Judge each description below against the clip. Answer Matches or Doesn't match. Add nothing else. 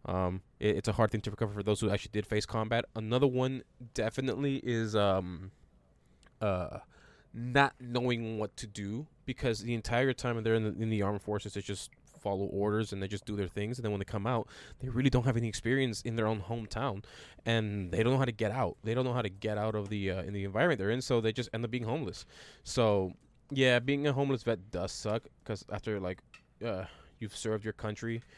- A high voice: Doesn't match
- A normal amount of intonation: Matches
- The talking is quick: Matches